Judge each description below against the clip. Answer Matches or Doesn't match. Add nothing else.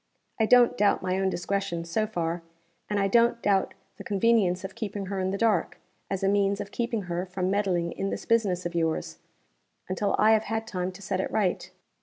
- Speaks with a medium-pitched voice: Doesn't match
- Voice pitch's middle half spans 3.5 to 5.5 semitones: Doesn't match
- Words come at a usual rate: Doesn't match